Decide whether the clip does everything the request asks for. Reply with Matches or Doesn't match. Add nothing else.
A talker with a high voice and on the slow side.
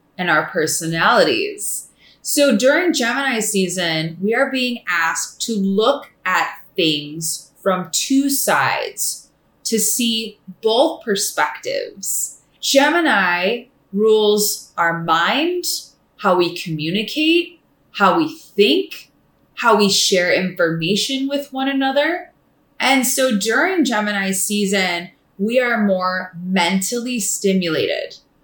Matches